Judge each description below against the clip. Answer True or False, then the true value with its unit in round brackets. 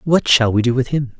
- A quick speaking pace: True (300 wpm)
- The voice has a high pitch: False (130 Hz)